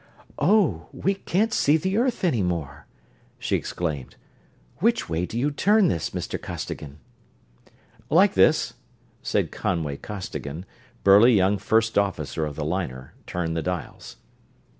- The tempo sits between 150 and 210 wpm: No, slow, 135 wpm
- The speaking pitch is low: Yes, very low, 95 Hz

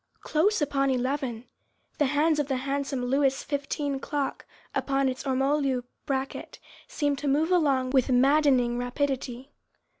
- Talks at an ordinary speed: No, slow, 130 wpm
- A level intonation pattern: Yes, narrow, 1.9 semitones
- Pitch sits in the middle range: No, very high, 275 Hz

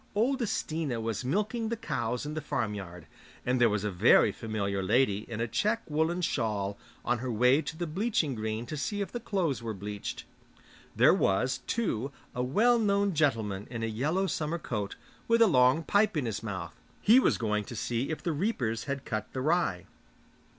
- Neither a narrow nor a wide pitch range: No, wide, 8.0 semitones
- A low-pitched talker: Yes, low, 130 Hz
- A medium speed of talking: Yes, average, 190 wpm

